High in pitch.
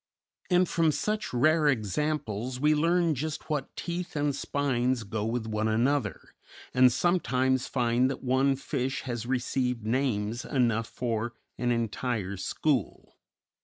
No: low, 130 Hz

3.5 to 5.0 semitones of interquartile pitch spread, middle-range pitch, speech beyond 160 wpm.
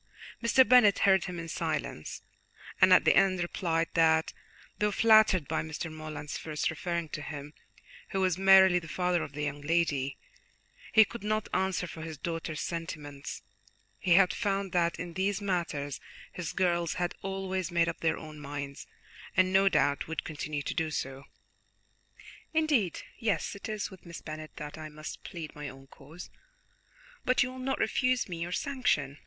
Yes: average, 3.9 semitones; medium, 170 Hz; average, 170 wpm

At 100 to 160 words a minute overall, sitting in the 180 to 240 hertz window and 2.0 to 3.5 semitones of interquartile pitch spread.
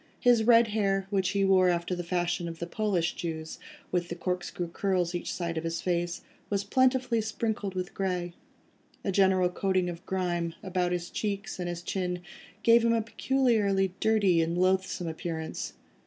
No: average, 170 wpm; medium, 185 Hz; narrow, 2.6 semitones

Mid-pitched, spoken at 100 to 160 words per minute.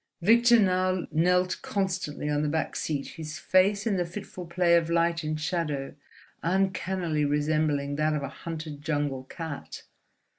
Yes: medium, 165 Hz; average, 150 wpm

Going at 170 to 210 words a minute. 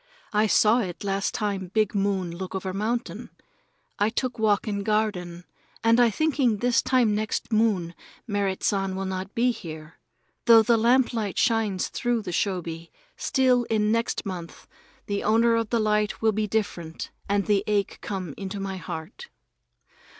No: average, 160 wpm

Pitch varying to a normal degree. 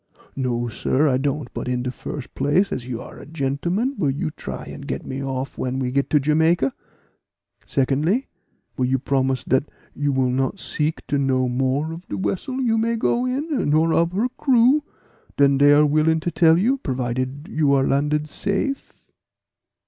Yes: average, 4.6 semitones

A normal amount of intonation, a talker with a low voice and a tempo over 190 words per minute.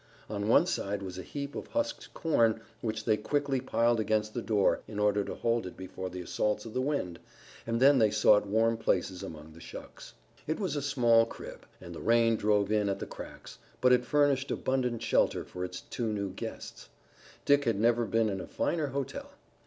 Yes: average, 4.1 semitones; low, 115 Hz; fast, 205 wpm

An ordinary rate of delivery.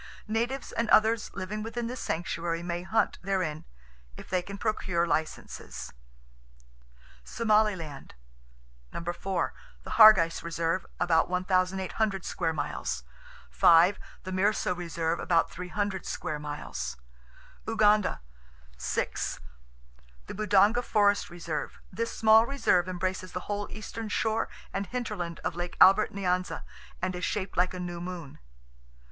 No: slow, 110 wpm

